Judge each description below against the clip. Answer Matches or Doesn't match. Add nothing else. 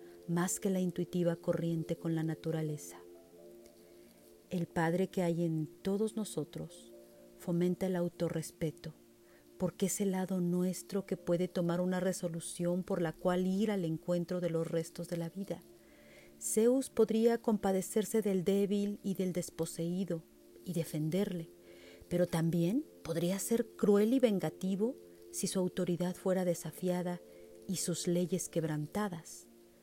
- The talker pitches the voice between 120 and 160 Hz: Doesn't match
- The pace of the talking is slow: Doesn't match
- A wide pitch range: Doesn't match